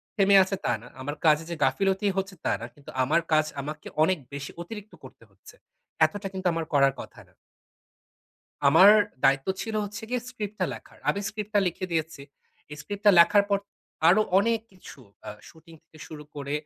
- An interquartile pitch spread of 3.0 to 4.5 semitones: No, average, 5.1 semitones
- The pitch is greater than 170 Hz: Yes, medium, 185 Hz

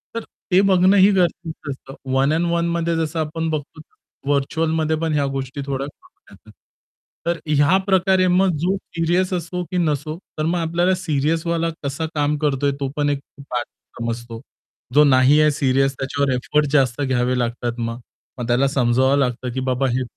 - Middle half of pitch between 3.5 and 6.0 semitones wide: Yes, average, 3.9 semitones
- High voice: No, medium, 150 Hz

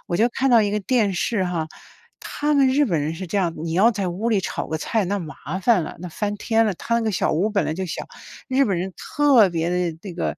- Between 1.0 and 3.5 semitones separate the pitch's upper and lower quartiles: No, average, 4.8 semitones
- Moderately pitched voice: No, high, 200 Hz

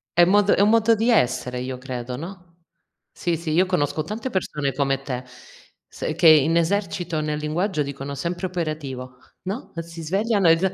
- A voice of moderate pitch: Yes, medium, 165 Hz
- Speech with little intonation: No, average, 5.0 semitones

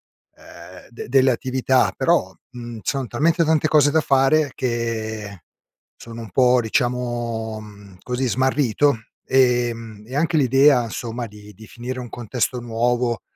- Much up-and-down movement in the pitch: No, average, 2.7 semitones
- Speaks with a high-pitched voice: No, low, 120 Hz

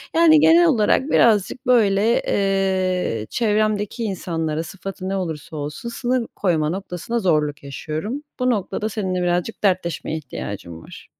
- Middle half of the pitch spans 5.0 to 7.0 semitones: Yes, wide, 5.6 semitones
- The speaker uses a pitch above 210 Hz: No, high, 195 Hz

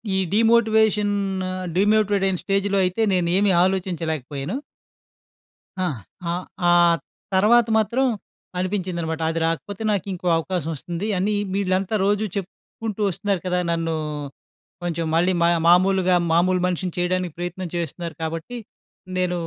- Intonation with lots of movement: No, average, 2.9 semitones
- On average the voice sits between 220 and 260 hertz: No, medium, 185 Hz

